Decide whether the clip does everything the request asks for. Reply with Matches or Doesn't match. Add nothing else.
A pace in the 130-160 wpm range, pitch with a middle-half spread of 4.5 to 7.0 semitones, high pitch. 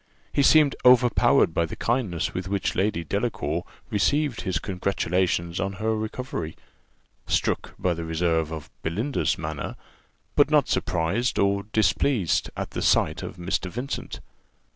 Doesn't match